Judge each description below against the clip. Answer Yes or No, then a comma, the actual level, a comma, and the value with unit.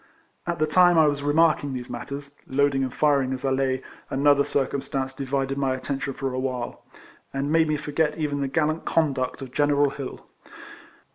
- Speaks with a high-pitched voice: No, medium, 140 Hz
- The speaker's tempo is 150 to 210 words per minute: Yes, average, 185 wpm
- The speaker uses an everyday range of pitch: No, narrow, 1.8 semitones